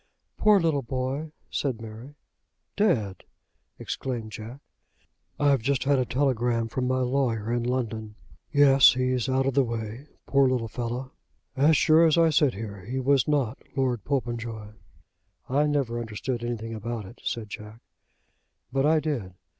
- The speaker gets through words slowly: No, average, 150 wpm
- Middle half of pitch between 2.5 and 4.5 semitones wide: Yes, average, 3.4 semitones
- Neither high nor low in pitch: No, low, 125 Hz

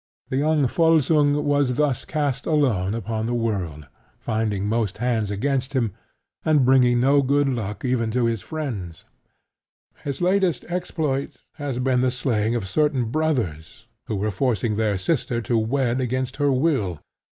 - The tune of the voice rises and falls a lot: No, average, 4.5 semitones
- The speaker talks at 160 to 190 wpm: No, average, 150 wpm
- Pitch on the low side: Yes, low, 125 Hz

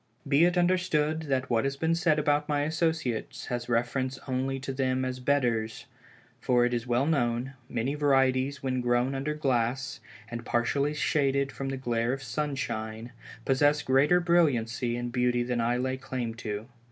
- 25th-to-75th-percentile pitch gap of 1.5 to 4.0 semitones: Yes, average, 3.0 semitones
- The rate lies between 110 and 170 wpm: Yes, average, 165 wpm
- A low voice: Yes, low, 130 Hz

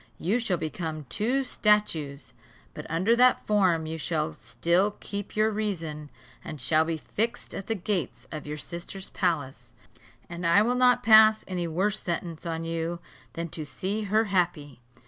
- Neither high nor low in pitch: Yes, medium, 175 Hz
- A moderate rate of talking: Yes, average, 165 wpm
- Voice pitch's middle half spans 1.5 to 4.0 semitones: No, average, 4.8 semitones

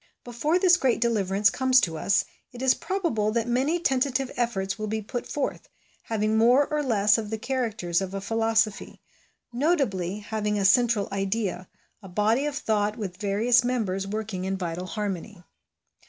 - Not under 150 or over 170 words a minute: Yes, average, 165 wpm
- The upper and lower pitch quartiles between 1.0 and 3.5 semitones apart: No, average, 3.9 semitones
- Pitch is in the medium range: No, high, 220 Hz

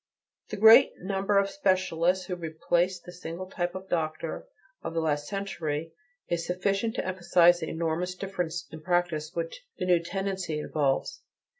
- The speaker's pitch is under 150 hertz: No, medium, 175 Hz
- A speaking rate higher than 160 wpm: No, average, 155 wpm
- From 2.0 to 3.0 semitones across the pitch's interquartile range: Yes, average, 2.7 semitones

